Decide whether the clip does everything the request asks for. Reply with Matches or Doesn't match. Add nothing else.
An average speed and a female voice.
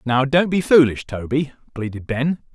Doesn't match